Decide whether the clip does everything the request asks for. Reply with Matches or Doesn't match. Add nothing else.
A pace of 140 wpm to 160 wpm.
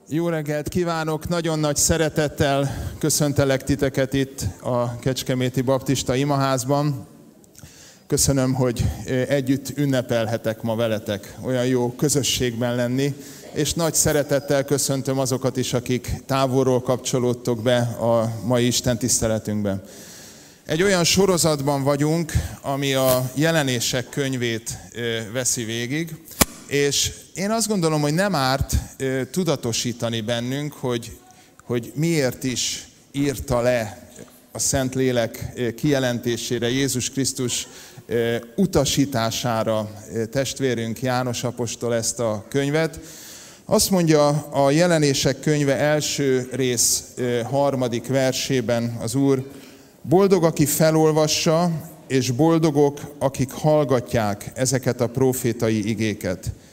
Doesn't match